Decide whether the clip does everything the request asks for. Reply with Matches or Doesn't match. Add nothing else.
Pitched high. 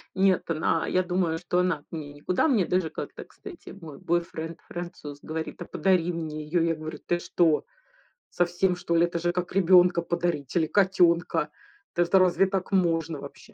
Doesn't match